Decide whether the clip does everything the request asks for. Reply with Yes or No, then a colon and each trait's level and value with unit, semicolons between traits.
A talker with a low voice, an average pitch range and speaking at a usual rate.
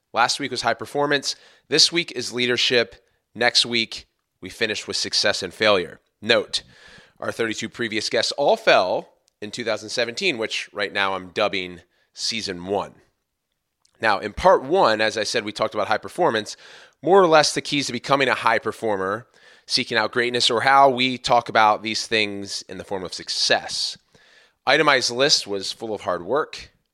Yes: low, 115 Hz; average, 3.8 semitones; average, 170 wpm